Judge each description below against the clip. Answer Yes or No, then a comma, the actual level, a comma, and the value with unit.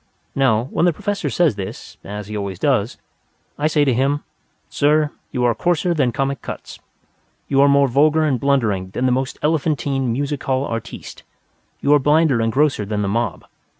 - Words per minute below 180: No, average, 185 wpm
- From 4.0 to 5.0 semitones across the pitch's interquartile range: Yes, average, 4.3 semitones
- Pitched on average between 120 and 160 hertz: Yes, low, 135 Hz